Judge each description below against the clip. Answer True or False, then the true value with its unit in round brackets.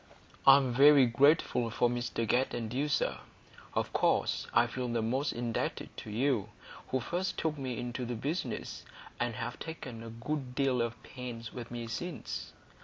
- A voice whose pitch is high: False (125 Hz)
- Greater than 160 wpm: True (170 wpm)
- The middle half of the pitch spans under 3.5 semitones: True (2.8 semitones)